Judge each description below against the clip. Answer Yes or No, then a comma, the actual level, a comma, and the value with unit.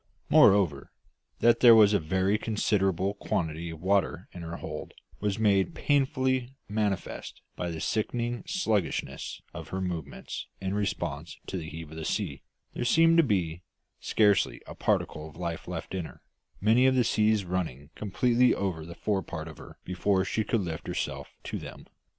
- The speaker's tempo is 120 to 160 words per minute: No, average, 170 wpm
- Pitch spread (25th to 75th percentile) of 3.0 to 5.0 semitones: Yes, average, 4.6 semitones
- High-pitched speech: No, very low, 95 Hz